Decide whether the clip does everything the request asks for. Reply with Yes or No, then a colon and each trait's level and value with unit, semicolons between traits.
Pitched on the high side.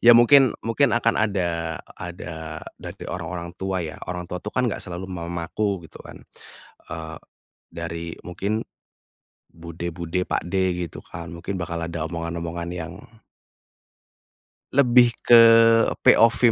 No: very low, 90 Hz